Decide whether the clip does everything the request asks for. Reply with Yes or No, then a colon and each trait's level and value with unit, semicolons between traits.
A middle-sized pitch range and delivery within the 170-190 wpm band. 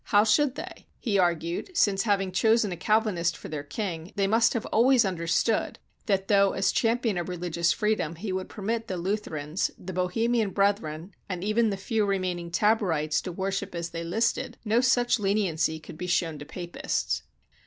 Yes: average, 4.1 semitones; average, 180 wpm